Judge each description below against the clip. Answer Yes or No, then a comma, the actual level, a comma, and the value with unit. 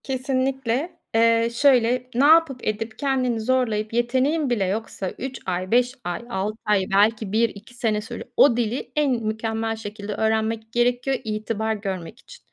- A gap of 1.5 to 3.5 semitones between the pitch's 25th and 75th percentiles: Yes, average, 3.0 semitones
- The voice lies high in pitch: Yes, high, 230 Hz